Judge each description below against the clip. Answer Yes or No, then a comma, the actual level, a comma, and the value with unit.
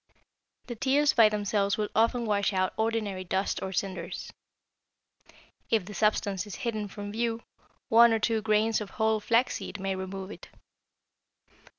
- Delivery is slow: No, average, 150 wpm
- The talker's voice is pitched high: Yes, high, 210 Hz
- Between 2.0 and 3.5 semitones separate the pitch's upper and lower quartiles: Yes, narrow, 2.5 semitones